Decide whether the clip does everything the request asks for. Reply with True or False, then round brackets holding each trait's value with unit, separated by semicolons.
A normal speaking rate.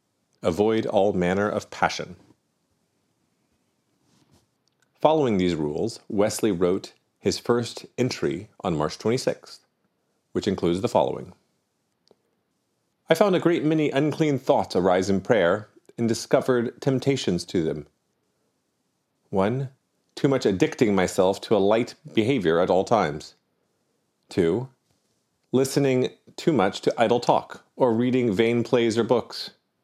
False (120 wpm)